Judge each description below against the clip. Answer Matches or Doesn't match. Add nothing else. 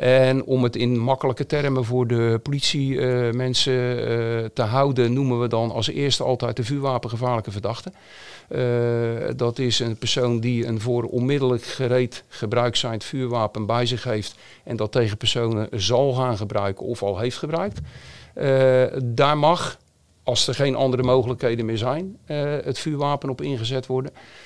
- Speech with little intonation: Matches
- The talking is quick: Doesn't match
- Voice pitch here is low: Matches